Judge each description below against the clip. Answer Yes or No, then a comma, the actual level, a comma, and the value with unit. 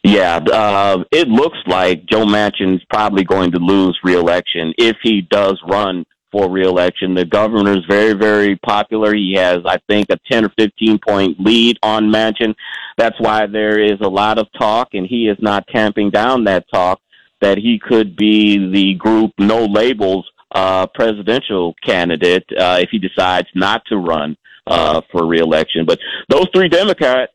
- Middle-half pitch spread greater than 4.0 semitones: No, average, 2.8 semitones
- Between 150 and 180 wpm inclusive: Yes, average, 165 wpm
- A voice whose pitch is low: Yes, low, 105 Hz